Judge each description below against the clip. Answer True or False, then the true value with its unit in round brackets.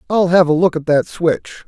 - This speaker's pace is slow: False (250 wpm)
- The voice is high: False (165 Hz)